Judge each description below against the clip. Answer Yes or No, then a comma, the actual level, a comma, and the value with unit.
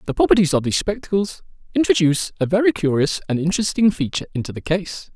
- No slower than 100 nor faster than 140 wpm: No, average, 175 wpm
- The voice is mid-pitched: Yes, medium, 175 Hz